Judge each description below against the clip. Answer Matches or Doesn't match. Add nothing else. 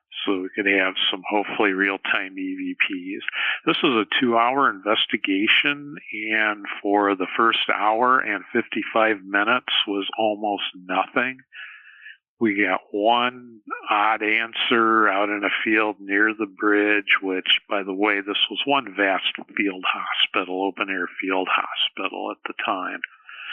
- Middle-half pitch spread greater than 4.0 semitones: Doesn't match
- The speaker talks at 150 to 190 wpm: Doesn't match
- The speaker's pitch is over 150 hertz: Doesn't match